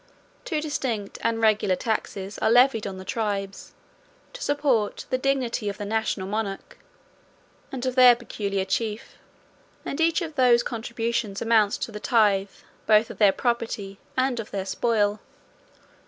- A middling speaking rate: Yes, average, 150 wpm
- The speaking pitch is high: Yes, high, 225 Hz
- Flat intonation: No, average, 3.4 semitones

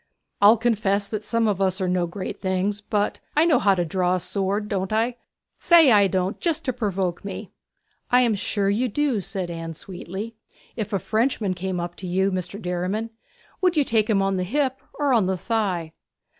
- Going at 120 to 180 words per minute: No, average, 200 wpm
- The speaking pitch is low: No, high, 200 Hz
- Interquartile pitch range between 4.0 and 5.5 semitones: No, average, 3.5 semitones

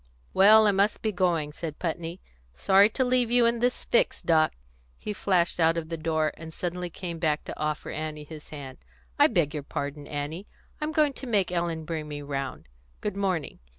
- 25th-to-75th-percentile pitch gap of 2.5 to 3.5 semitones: No, average, 4.6 semitones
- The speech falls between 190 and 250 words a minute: Yes, average, 195 wpm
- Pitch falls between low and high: Yes, medium, 170 Hz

